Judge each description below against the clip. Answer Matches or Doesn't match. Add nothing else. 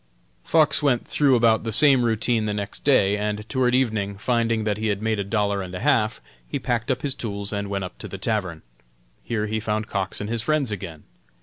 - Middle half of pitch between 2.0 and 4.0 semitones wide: Matches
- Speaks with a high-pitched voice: Doesn't match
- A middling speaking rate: Doesn't match